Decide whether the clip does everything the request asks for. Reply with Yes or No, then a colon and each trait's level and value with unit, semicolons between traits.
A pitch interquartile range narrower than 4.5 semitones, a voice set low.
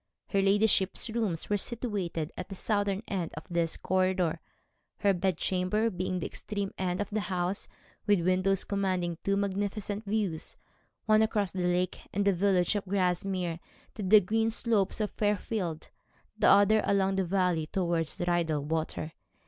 No: narrow, 2.5 semitones; high, 190 Hz